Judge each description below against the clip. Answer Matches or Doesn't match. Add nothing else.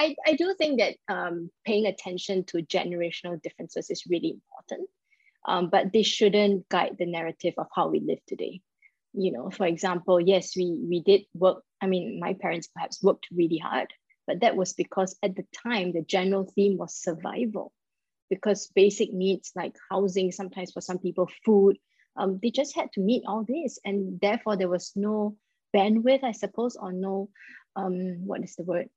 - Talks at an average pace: Matches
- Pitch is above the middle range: Matches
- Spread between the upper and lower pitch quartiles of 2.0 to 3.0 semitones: Matches